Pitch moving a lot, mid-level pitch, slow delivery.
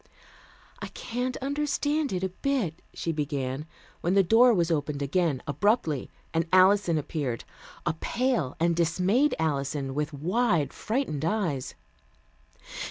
Yes: wide, 7.1 semitones; medium, 170 Hz; slow, 125 wpm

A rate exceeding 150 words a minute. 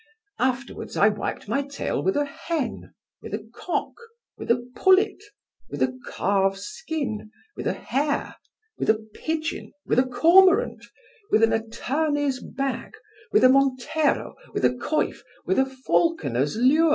No: average, 145 wpm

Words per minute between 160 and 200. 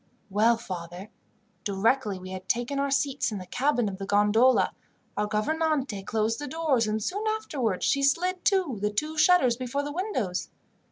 Yes: average, 170 wpm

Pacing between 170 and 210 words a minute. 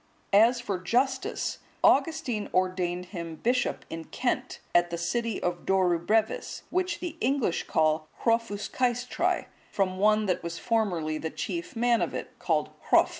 No: average, 140 wpm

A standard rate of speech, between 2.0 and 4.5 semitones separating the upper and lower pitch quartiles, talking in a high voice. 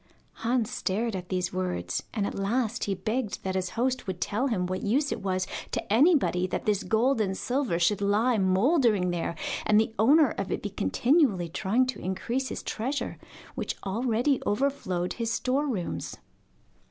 No: average, 175 wpm; average, 5.2 semitones; high, 215 Hz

